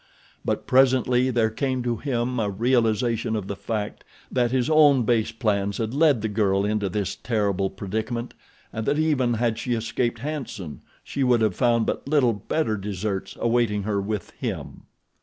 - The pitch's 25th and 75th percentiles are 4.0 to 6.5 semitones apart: No, average, 3.3 semitones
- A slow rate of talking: No, average, 170 wpm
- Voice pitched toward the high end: No, low, 115 Hz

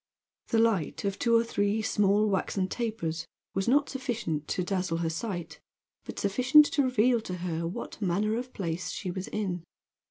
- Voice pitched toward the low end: No, high, 200 Hz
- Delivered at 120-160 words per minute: No, average, 170 wpm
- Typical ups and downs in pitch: Yes, average, 4.5 semitones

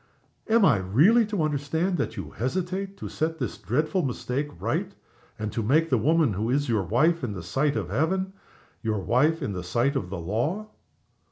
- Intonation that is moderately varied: No, wide, 7.1 semitones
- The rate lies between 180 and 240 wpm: Yes, average, 190 wpm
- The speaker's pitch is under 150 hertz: Yes, medium, 140 Hz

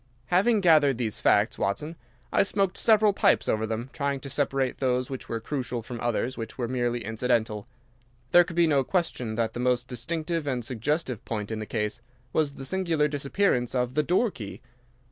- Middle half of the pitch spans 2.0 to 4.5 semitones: No, average, 5.2 semitones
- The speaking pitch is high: No, low, 130 Hz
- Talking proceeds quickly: No, average, 185 wpm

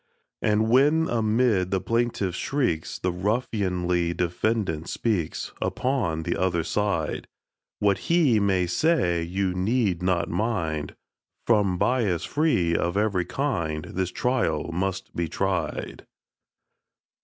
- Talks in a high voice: No, very low, 95 Hz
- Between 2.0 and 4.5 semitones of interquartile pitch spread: No, average, 4.9 semitones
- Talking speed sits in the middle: No, slow, 115 wpm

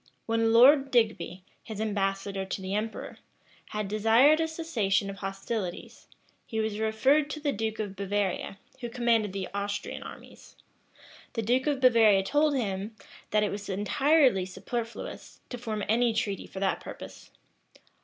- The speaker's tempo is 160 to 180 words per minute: No, average, 150 wpm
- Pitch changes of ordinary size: Yes, average, 3.6 semitones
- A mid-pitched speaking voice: No, high, 220 Hz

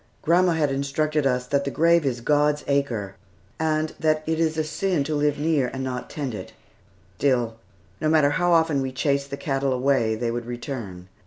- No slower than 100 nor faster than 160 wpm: No, average, 190 wpm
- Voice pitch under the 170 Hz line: Yes, medium, 140 Hz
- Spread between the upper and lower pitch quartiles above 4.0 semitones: No, average, 3.4 semitones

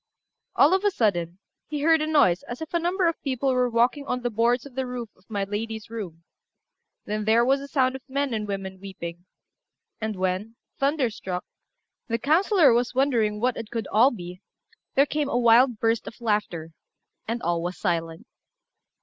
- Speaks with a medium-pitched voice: No, high, 230 Hz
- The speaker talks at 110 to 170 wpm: No, average, 185 wpm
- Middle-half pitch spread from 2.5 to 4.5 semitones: No, average, 5.3 semitones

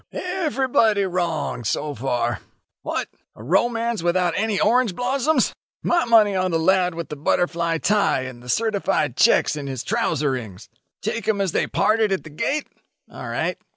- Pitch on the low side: No, medium, 185 Hz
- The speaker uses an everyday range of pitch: No, wide, 7.1 semitones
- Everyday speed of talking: Yes, average, 170 wpm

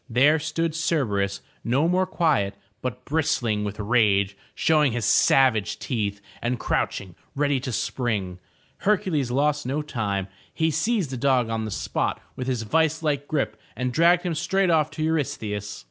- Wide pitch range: Yes, wide, 6.2 semitones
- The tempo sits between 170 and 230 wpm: No, average, 160 wpm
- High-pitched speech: No, low, 135 Hz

